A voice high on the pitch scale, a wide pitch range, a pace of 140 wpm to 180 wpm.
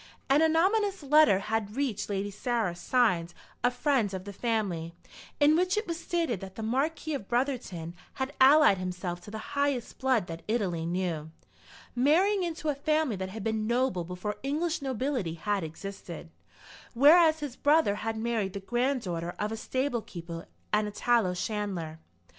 Yes: high, 225 Hz; wide, 7.2 semitones; average, 165 wpm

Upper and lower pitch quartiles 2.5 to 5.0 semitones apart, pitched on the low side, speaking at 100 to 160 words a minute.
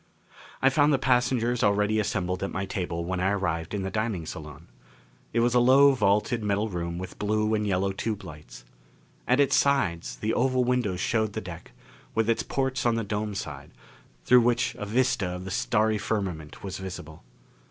No: average, 4.6 semitones; low, 105 Hz; average, 185 wpm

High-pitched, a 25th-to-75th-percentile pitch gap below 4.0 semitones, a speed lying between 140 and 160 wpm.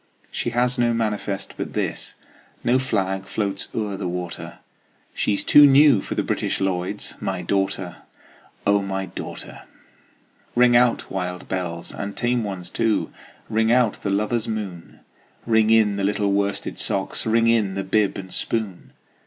No: low, 100 Hz; average, 3.0 semitones; average, 155 wpm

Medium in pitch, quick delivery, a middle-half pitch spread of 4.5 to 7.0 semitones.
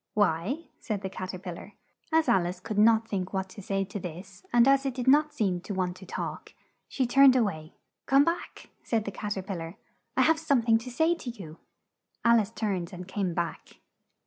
No: high, 205 Hz; fast, 225 wpm; average, 5.0 semitones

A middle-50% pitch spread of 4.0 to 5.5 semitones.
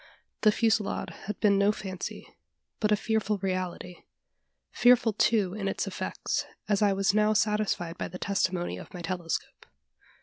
No: narrow, 2.4 semitones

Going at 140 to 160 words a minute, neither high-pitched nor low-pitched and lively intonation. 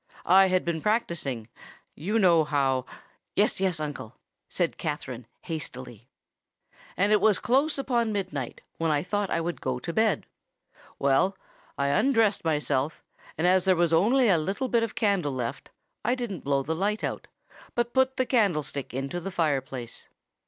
Yes: average, 155 wpm; medium, 175 Hz; wide, 6.8 semitones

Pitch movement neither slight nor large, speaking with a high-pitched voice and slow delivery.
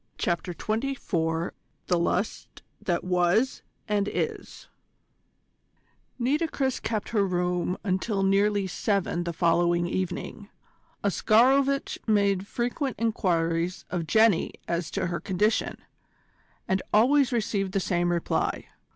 Yes: average, 4.1 semitones; high, 195 Hz; slow, 110 wpm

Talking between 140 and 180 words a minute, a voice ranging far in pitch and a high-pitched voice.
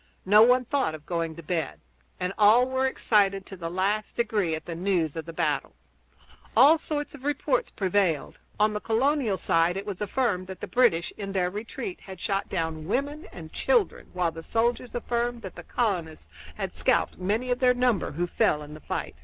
No: average, 195 wpm; wide, 6.1 semitones; high, 200 Hz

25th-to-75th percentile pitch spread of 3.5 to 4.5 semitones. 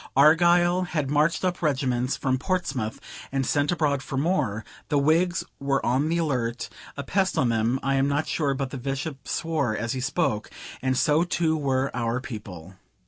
Yes: average, 3.8 semitones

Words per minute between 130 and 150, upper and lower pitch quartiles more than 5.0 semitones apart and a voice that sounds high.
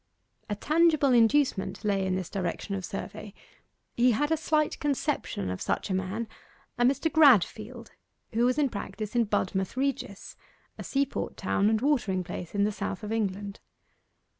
No: average, 165 wpm; wide, 5.6 semitones; high, 220 Hz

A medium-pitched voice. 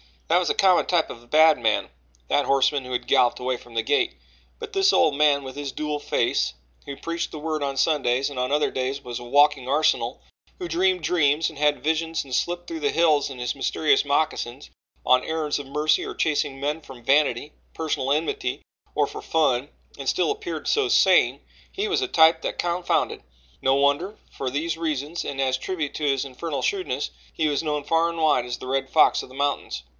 Yes: medium, 145 Hz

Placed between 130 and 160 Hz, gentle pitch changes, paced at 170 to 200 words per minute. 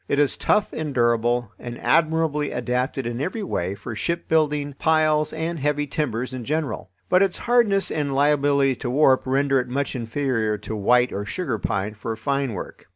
No: medium, 140 Hz; average, 4.2 semitones; average, 175 wpm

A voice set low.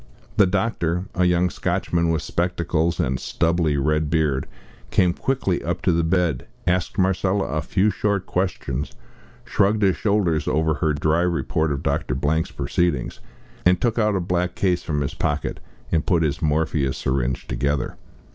Yes: very low, 85 Hz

